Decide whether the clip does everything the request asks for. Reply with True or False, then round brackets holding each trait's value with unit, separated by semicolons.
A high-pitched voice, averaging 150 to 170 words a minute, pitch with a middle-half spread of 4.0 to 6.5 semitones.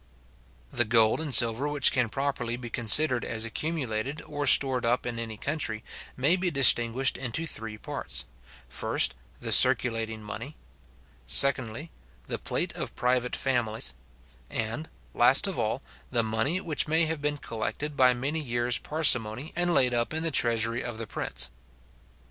False (125 Hz; 155 wpm; 4.3 semitones)